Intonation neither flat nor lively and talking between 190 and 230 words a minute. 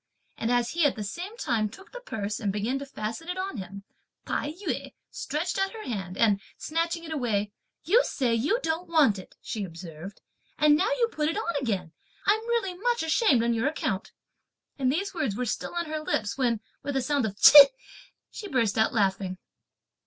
No: wide, 8.2 semitones; average, 200 wpm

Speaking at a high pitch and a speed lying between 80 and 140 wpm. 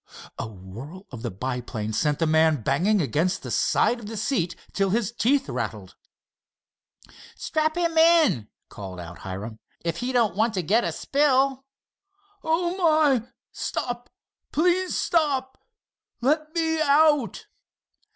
Yes: high, 235 Hz; slow, 135 wpm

